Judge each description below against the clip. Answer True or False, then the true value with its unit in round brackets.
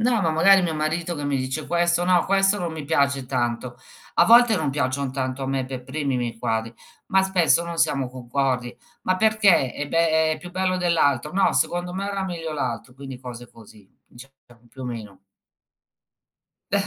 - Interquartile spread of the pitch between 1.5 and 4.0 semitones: False (5.3 semitones)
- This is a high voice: False (145 Hz)